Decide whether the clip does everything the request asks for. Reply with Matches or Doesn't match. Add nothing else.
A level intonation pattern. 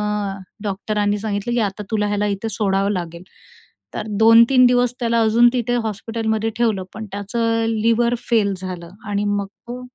Matches